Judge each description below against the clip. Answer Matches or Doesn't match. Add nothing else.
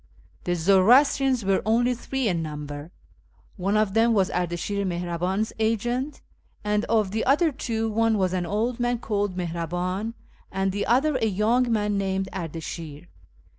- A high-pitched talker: Matches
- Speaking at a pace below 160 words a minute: Matches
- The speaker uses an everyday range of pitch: Matches